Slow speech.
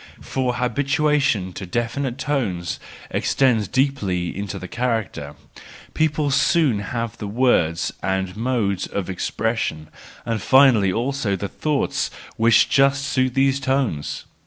Yes: slow, 115 wpm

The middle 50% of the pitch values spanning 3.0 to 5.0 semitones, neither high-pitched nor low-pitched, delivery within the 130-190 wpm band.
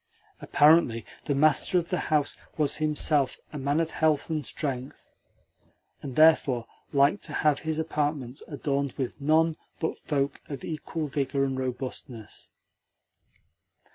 No: narrow, 2.5 semitones; medium, 145 Hz; slow, 135 wpm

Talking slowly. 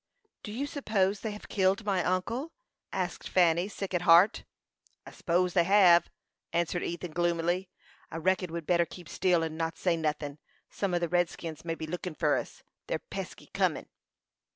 No: average, 175 wpm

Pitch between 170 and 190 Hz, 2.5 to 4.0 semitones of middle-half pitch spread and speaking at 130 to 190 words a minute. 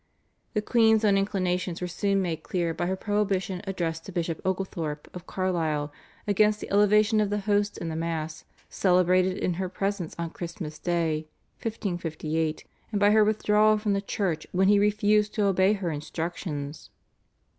Yes: medium, 185 Hz; average, 3.6 semitones; average, 165 wpm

